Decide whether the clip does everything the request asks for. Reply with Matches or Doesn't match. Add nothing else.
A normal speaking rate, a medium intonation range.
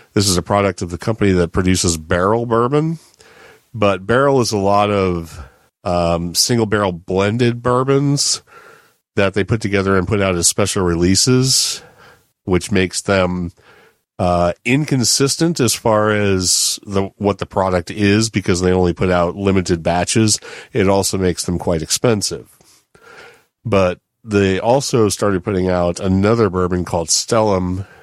Matches